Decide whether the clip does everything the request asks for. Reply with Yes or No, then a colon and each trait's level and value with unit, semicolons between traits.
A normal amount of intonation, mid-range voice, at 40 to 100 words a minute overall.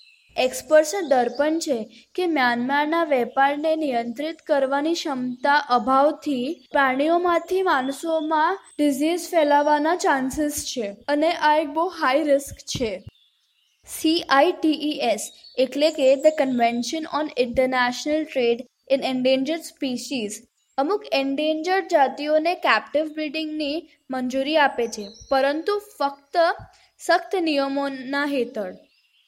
No: average, 3.3 semitones; very high, 290 Hz; average, 95 wpm